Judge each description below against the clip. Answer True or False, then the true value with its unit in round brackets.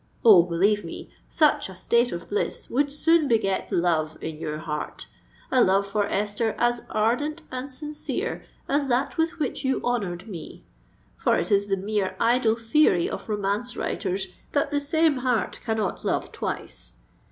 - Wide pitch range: True (5.7 semitones)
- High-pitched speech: True (220 Hz)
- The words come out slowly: False (160 wpm)